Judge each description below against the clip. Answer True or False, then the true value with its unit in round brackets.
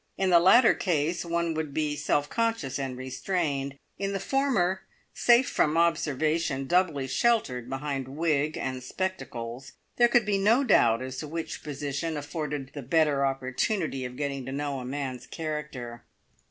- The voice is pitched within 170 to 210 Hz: False (150 Hz)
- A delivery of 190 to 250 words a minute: False (155 wpm)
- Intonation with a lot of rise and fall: False (4.7 semitones)